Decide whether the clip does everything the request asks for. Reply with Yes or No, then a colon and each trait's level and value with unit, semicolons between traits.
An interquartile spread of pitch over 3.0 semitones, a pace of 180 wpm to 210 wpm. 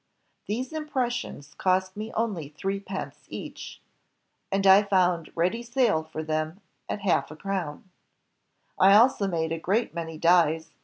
No: average, 4.6 semitones; average, 145 wpm